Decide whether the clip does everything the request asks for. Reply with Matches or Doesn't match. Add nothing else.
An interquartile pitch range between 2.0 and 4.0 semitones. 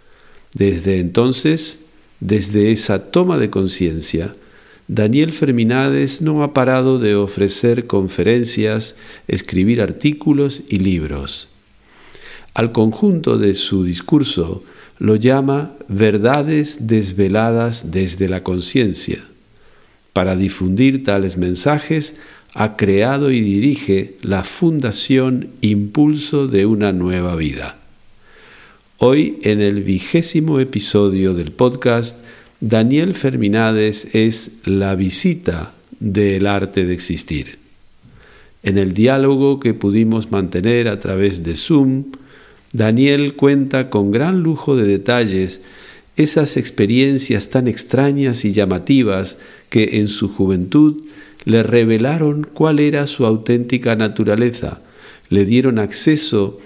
Doesn't match